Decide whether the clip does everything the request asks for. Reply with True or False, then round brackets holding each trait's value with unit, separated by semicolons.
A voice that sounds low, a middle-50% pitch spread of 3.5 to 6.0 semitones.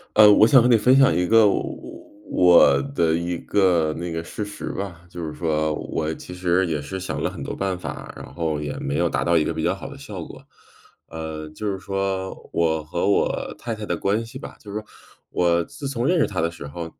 True (90 Hz; 4.2 semitones)